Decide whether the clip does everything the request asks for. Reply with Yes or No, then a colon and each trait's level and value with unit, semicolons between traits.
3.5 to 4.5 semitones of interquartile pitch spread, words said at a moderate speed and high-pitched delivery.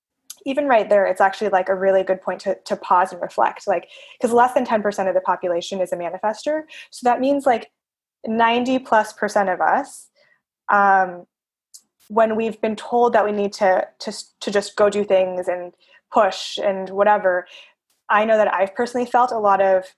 Yes: average, 3.9 semitones; average, 190 wpm; high, 205 Hz